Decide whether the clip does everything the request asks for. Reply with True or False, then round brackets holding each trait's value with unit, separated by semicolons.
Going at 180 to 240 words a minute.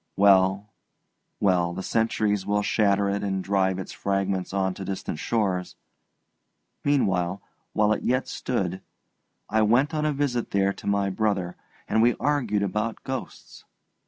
False (145 wpm)